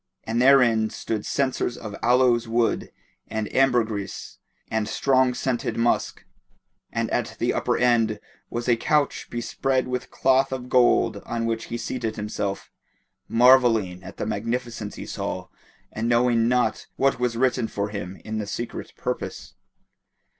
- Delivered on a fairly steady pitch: Yes, narrow, 2.3 semitones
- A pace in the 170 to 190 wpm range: No, average, 145 wpm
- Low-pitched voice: Yes, low, 120 Hz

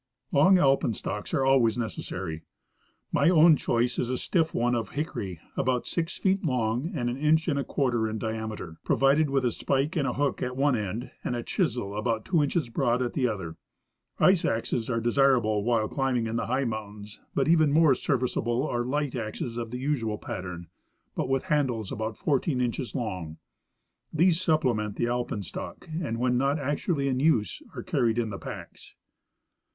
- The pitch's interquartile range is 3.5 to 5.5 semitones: Yes, average, 4.2 semitones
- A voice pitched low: Yes, low, 125 Hz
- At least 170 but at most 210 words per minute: Yes, average, 180 wpm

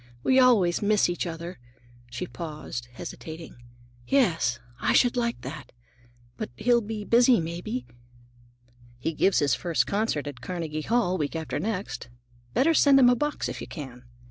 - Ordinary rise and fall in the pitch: No, wide, 7.5 semitones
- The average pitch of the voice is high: No, medium, 175 Hz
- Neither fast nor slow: Yes, average, 155 wpm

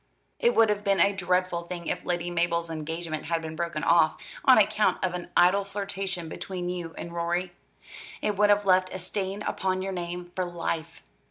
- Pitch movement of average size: No, narrow, 2.3 semitones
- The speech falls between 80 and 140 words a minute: No, average, 190 wpm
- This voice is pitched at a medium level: Yes, medium, 180 Hz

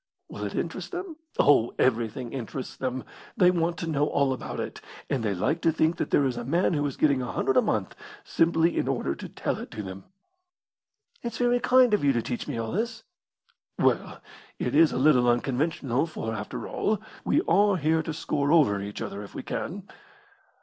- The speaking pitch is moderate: Yes, medium, 145 Hz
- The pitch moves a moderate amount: No, wide, 5.8 semitones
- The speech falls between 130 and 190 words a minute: No, fast, 205 wpm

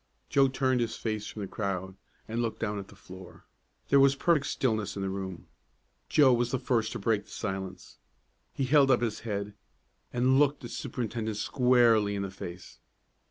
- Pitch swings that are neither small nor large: Yes, average, 4.5 semitones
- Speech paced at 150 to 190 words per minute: Yes, average, 185 wpm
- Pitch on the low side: Yes, low, 115 Hz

